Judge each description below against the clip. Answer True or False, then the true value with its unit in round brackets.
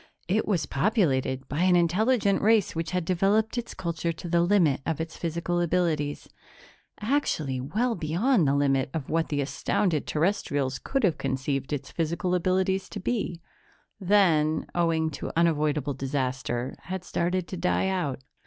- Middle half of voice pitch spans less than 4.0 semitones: False (4.3 semitones)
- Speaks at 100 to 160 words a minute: True (155 wpm)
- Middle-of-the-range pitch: True (170 Hz)